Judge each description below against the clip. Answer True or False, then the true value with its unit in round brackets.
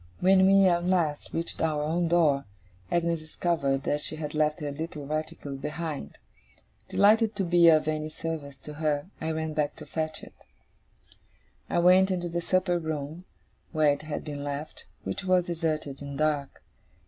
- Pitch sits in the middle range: True (155 Hz)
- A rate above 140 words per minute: True (170 wpm)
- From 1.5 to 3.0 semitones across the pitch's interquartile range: True (2.6 semitones)